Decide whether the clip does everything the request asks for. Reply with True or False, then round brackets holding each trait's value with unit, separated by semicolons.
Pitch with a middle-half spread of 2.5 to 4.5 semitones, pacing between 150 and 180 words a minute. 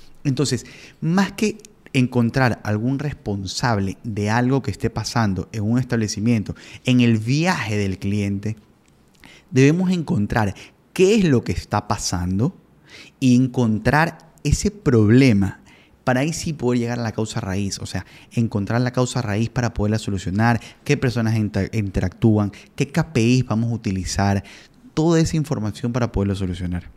False (4.2 semitones; 140 wpm)